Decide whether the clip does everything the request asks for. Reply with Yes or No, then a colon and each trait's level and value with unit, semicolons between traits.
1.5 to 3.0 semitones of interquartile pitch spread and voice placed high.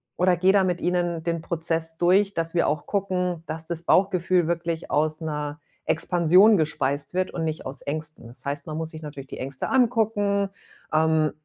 No: average, 2.7 semitones; medium, 165 Hz